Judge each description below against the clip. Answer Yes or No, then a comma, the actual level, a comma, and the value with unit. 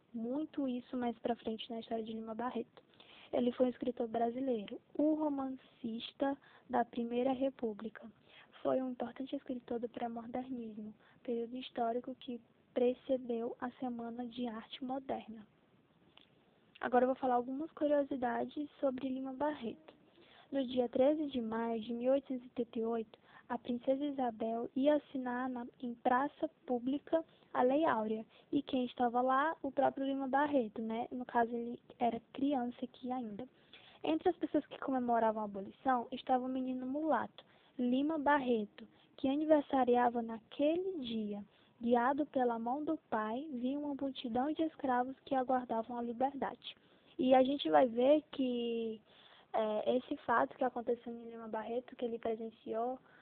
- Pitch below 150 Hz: No, very high, 250 Hz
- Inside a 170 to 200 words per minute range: No, average, 145 wpm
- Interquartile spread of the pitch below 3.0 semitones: Yes, narrow, 2.5 semitones